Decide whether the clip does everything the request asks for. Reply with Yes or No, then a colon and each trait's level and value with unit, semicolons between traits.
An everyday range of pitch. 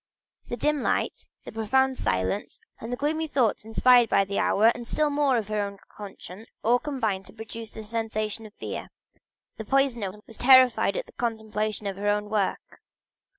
Yes: average, 3.5 semitones